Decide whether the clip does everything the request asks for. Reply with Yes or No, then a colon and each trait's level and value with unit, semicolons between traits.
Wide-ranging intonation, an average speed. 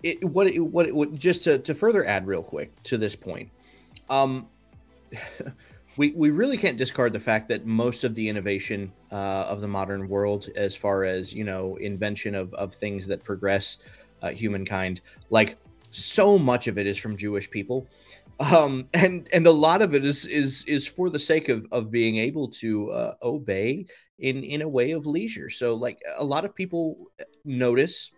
Yes: wide, 7.0 semitones; average, 185 wpm